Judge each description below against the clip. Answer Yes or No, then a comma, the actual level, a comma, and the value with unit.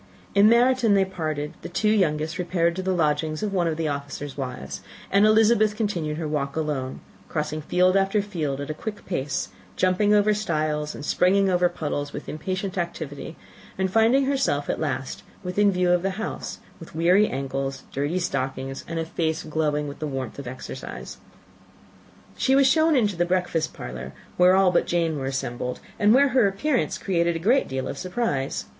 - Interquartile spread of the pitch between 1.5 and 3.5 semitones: No, average, 5.2 semitones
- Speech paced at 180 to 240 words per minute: Yes, average, 185 wpm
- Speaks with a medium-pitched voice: Yes, medium, 170 Hz